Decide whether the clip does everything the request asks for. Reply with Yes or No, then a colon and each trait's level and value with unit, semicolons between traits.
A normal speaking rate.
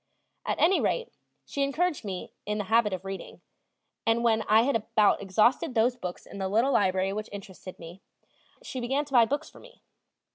Yes: average, 190 wpm